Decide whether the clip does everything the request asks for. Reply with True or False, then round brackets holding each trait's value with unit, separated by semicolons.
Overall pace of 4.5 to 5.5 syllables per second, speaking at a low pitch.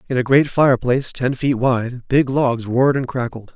True (5.0 syllables/s; 130 Hz)